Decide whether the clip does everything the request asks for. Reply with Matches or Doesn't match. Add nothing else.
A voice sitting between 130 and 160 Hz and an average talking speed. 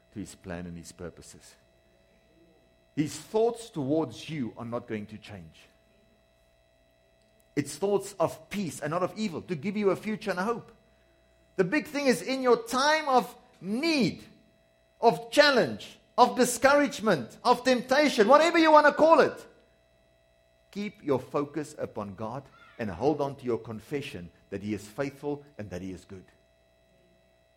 Matches